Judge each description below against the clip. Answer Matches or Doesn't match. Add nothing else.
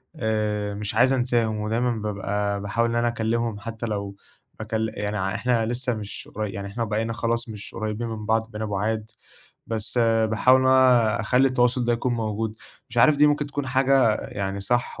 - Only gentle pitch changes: Matches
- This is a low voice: Matches